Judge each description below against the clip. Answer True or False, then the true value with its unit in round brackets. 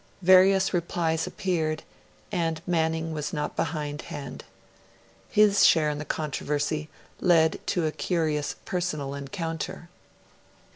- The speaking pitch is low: False (160 Hz)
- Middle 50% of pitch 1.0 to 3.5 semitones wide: True (2.8 semitones)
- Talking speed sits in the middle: False (105 wpm)